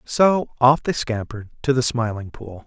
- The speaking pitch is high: No, low, 120 Hz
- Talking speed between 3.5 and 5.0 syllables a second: Yes, 4.7 syllables/s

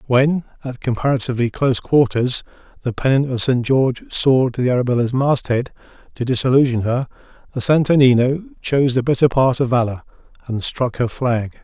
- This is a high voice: No, low, 125 Hz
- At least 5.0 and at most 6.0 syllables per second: Yes, 5.7 syllables/s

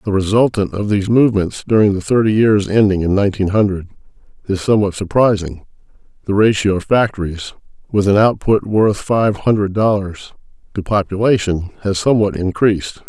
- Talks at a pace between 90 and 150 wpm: Yes, average, 145 wpm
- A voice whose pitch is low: Yes, low, 100 Hz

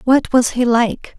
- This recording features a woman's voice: Yes, female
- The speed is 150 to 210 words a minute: Yes, fast, 205 wpm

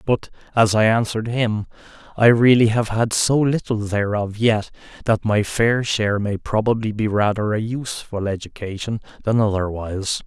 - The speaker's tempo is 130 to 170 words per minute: Yes, average, 150 wpm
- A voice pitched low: Yes, low, 110 Hz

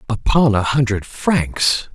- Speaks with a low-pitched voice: Yes, low, 120 Hz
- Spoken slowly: Yes, slow, 125 wpm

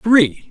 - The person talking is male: Yes, male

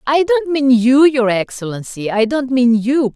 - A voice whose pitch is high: Yes, very high, 255 Hz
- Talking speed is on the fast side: No, average, 190 wpm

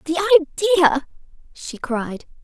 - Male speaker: No, female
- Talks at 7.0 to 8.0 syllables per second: No, 4.8 syllables/s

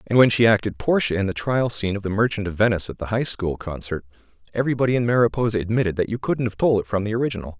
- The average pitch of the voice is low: Yes, low, 110 Hz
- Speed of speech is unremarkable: No, fast, 255 wpm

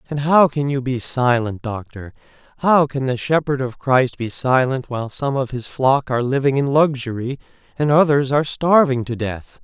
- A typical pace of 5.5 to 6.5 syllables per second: No, 4.9 syllables/s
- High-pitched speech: No, low, 130 Hz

